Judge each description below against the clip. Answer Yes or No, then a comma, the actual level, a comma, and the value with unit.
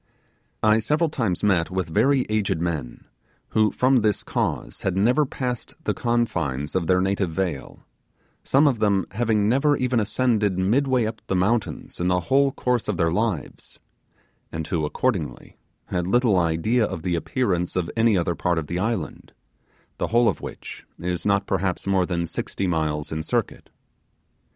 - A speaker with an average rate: Yes, average, 165 wpm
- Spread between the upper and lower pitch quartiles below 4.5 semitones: No, wide, 5.4 semitones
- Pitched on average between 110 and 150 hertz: No, low, 100 Hz